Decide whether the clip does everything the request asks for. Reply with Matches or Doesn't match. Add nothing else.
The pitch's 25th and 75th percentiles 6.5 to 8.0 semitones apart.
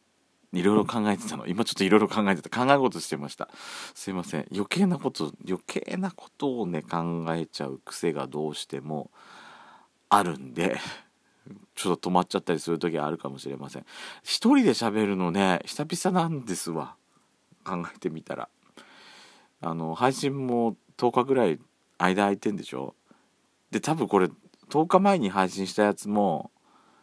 Matches